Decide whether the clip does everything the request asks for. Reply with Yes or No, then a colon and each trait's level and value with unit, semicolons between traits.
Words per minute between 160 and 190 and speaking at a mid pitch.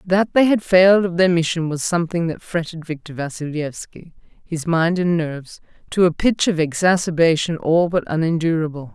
Yes: average, 170 wpm; medium, 170 Hz